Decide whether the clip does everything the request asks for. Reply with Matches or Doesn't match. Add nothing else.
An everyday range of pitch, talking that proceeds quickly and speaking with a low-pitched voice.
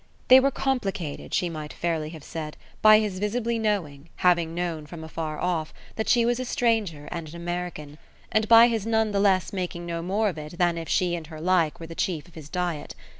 Doesn't match